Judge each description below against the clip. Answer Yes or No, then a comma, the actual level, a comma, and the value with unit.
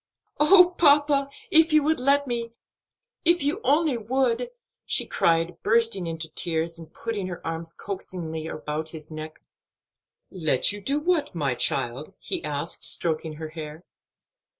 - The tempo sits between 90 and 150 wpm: Yes, average, 145 wpm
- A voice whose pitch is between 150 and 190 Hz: Yes, medium, 185 Hz